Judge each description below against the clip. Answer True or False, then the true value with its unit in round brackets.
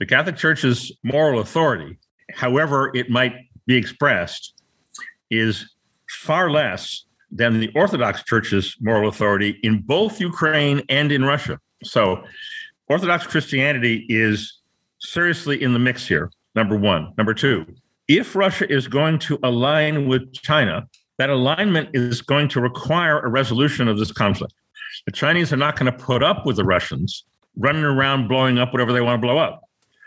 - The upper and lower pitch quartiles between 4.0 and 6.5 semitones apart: True (4.3 semitones)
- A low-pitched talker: True (130 Hz)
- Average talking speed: True (155 wpm)